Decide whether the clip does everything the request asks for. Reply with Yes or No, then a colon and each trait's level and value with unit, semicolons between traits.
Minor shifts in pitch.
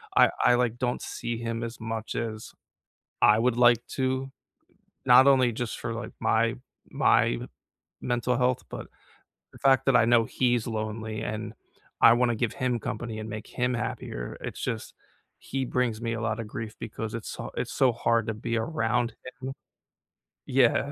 Yes: narrow, 1.9 semitones